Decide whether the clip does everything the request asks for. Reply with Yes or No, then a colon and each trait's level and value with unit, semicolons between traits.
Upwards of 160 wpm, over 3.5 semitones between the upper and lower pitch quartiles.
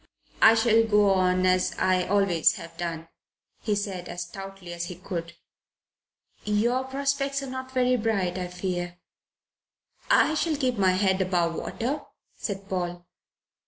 No: average, 145 wpm; average, 4.3 semitones